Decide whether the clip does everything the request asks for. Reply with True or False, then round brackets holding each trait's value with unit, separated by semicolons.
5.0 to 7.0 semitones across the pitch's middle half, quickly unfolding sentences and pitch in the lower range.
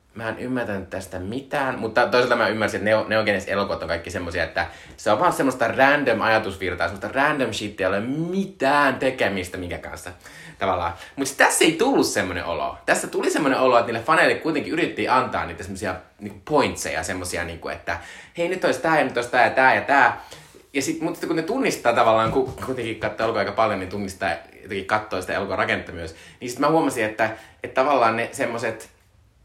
True (5.4 semitones; 200 wpm; 110 Hz)